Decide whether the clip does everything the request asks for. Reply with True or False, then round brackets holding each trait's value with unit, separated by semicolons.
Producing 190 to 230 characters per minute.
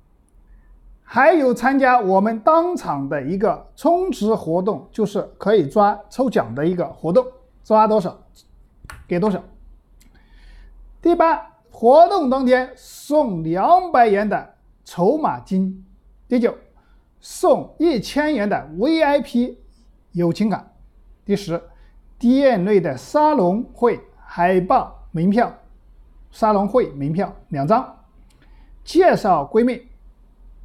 False (165 characters per minute)